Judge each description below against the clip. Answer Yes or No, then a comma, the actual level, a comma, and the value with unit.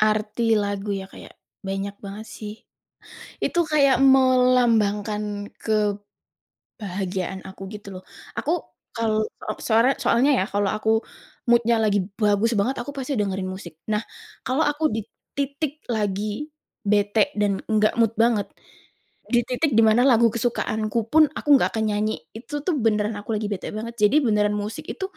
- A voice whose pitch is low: No, high, 215 Hz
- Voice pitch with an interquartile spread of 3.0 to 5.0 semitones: Yes, average, 3.4 semitones